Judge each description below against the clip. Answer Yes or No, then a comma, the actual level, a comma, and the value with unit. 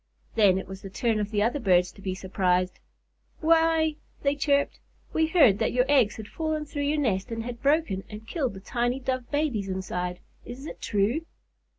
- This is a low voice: No, high, 235 Hz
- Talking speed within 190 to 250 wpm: Yes, average, 195 wpm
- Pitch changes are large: Yes, wide, 6.8 semitones